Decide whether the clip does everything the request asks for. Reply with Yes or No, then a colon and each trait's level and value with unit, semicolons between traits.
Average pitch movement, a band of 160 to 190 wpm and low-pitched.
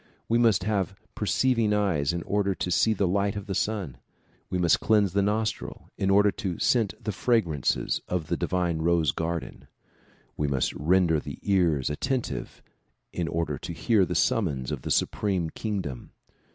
Yes: average, 4.0 semitones; average, 170 wpm; very low, 95 Hz